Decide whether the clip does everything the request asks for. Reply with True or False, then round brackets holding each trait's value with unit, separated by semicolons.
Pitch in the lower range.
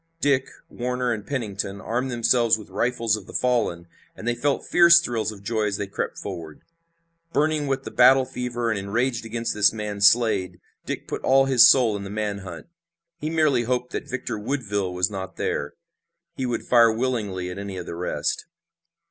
True (115 Hz)